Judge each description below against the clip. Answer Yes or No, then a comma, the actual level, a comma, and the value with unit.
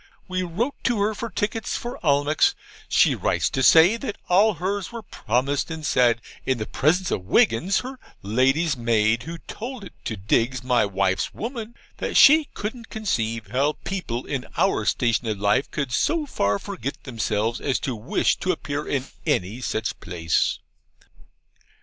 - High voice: No, medium, 140 Hz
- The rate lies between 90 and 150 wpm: No, average, 165 wpm